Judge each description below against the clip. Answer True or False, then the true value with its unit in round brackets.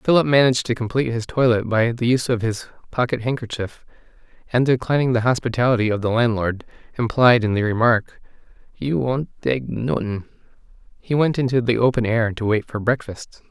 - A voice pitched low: True (120 Hz)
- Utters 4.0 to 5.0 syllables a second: False (5.6 syllables/s)